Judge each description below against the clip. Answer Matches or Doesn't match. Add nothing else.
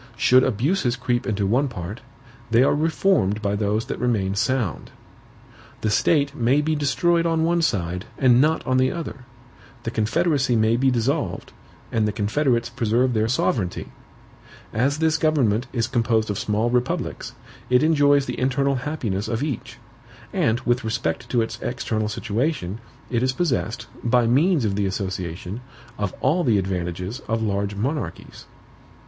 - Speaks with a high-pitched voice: Doesn't match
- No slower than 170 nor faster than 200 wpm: Doesn't match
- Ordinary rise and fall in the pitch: Matches